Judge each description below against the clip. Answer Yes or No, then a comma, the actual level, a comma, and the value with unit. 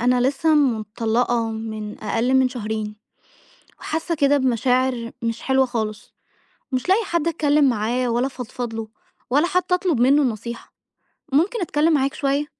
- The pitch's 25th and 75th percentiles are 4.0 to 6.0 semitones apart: Yes, average, 4.3 semitones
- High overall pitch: Yes, very high, 255 Hz